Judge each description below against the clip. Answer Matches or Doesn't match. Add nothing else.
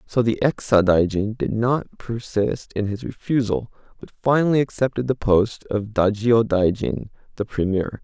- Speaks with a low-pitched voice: Matches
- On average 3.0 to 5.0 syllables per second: Matches